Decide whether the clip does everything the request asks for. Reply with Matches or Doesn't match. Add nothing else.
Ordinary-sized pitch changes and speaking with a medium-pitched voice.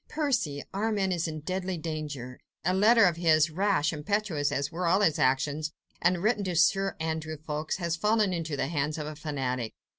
Matches